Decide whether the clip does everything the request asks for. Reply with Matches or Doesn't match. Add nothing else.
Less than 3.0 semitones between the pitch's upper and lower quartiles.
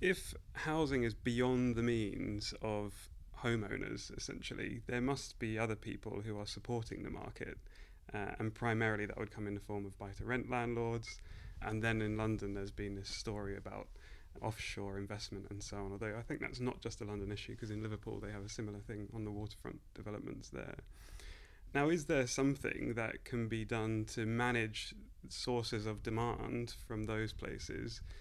Matches